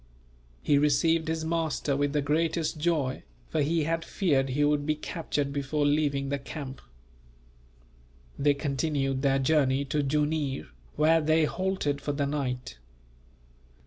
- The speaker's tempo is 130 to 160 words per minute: Yes, average, 140 wpm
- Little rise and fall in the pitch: Yes, narrow, 2.3 semitones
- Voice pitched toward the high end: No, medium, 145 Hz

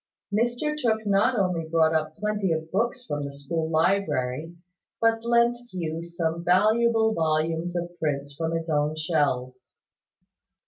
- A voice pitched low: No, medium, 170 Hz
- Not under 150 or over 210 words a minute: No, average, 140 wpm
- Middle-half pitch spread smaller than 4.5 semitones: No, average, 5.3 semitones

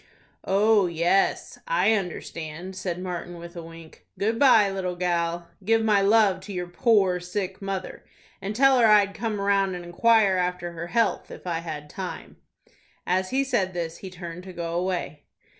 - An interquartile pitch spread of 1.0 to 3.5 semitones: Yes, average, 2.8 semitones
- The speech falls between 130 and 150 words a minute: No, average, 175 wpm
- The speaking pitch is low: No, medium, 185 Hz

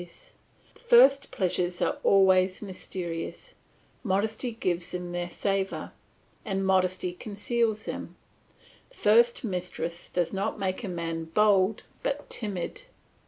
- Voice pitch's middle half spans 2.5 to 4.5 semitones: Yes, average, 3.4 semitones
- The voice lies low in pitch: No, high, 190 Hz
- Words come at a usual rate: No, slow, 115 wpm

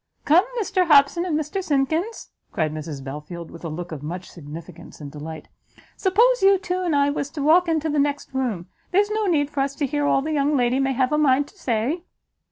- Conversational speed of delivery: No, fast, 220 wpm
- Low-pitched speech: No, very high, 285 Hz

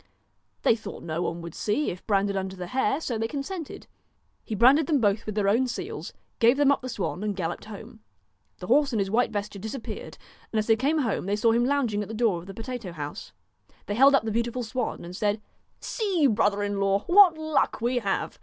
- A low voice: No, high, 225 Hz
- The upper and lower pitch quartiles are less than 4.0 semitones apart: No, average, 4.6 semitones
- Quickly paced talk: Yes, fast, 230 wpm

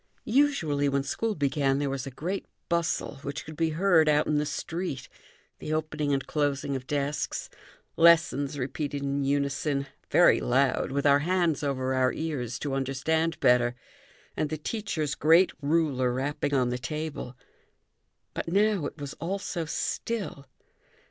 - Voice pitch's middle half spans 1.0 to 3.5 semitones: Yes, average, 2.9 semitones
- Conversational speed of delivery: Yes, average, 155 wpm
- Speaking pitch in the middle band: Yes, medium, 145 Hz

